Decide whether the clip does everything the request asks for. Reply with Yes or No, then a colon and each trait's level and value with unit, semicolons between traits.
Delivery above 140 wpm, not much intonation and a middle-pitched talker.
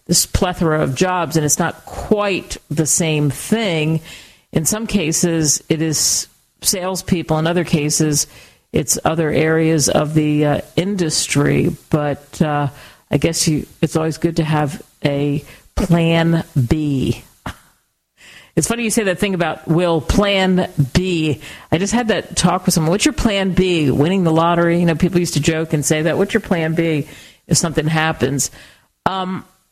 No: average, 165 wpm; average, 3.0 semitones; medium, 165 Hz